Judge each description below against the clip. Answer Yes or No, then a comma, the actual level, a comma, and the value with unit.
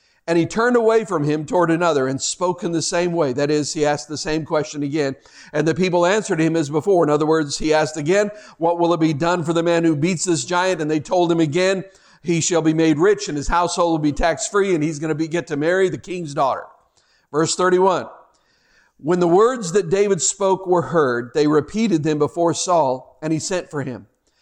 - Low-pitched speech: No, medium, 165 Hz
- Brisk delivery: Yes, fast, 235 wpm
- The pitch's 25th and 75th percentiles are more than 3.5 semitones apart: No, average, 2.7 semitones